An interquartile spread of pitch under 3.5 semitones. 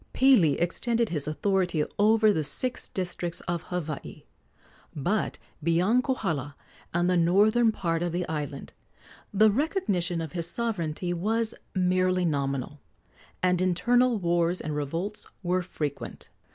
No: average, 4.4 semitones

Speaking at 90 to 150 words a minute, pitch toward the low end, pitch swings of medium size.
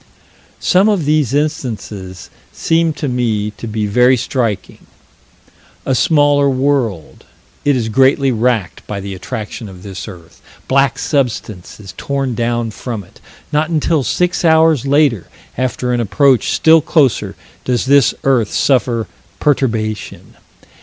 Yes: slow, 135 wpm; low, 125 Hz; average, 4.9 semitones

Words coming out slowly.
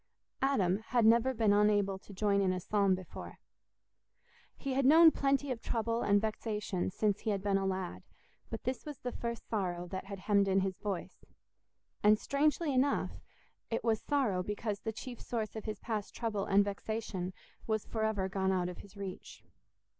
No: average, 185 wpm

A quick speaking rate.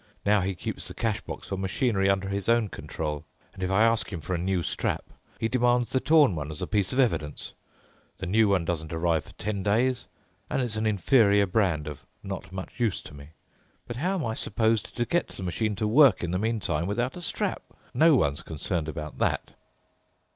Yes: fast, 210 wpm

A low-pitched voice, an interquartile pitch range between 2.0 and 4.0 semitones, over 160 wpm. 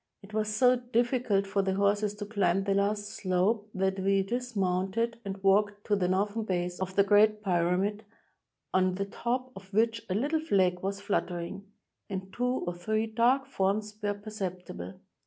No: high, 200 Hz; narrow, 2.4 semitones; average, 170 wpm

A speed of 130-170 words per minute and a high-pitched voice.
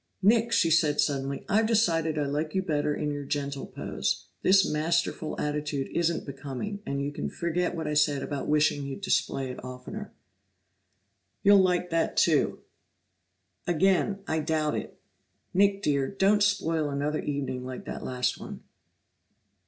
No: average, 150 wpm; medium, 155 Hz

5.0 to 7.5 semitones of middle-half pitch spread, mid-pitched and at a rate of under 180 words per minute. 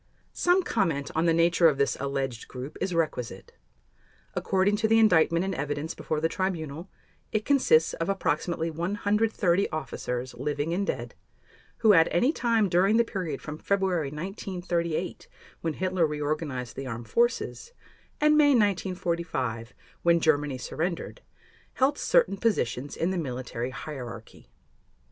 Yes: average, 5.3 semitones; medium, 170 Hz; average, 140 wpm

